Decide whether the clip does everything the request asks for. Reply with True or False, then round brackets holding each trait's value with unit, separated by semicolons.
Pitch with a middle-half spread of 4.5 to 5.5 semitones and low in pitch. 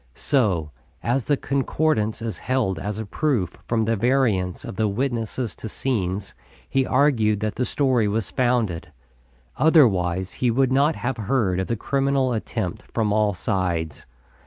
True (5.0 semitones; 115 Hz)